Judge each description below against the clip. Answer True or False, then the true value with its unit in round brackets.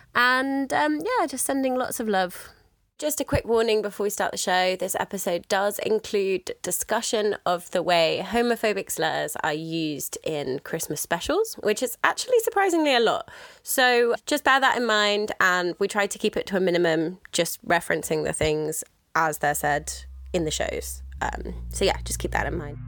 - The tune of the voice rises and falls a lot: True (7.5 semitones)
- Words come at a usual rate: True (185 wpm)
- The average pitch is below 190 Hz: False (205 Hz)